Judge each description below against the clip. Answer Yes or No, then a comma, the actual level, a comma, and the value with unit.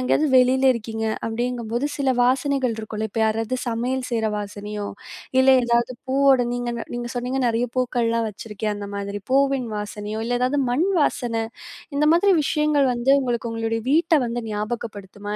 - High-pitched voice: Yes, high, 240 Hz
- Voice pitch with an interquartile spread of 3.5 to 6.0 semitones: No, average, 2.8 semitones